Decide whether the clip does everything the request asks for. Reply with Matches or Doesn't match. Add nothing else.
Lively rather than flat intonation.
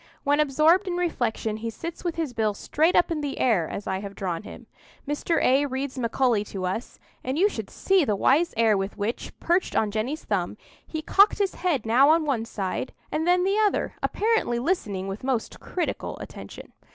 Matches